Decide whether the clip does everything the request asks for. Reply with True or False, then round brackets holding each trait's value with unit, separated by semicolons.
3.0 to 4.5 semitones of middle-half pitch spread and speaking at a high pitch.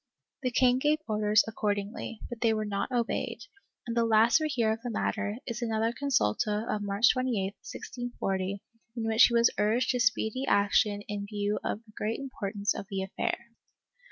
False (2.6 semitones; 220 Hz)